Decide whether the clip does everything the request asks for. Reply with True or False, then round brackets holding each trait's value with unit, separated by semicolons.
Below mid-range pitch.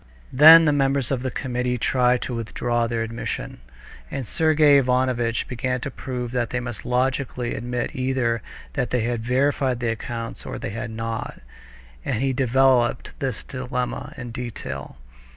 True (125 Hz)